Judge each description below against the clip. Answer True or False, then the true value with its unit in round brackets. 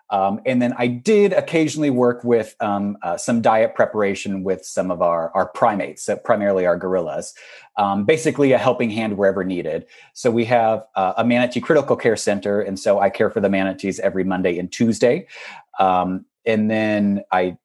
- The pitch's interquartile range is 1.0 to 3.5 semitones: False (4.1 semitones)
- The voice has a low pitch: True (105 Hz)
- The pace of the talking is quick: False (185 wpm)